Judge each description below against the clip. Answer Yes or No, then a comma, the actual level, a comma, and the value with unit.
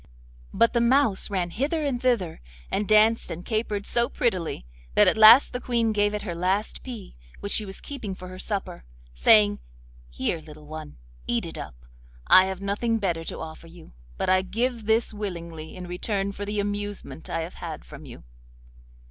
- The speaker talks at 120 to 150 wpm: No, average, 185 wpm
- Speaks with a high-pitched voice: Yes, high, 200 Hz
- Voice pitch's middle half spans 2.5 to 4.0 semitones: No, average, 4.6 semitones